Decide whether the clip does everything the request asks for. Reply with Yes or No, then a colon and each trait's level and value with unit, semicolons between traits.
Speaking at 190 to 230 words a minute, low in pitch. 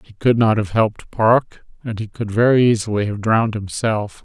Yes: average, 200 wpm; low, 110 Hz